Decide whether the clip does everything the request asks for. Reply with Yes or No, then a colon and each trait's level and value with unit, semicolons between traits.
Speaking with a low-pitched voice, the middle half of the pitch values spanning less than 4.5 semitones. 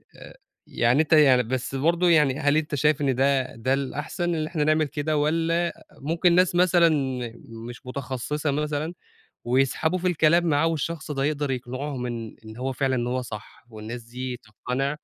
No: medium, 145 Hz; average, 3.7 semitones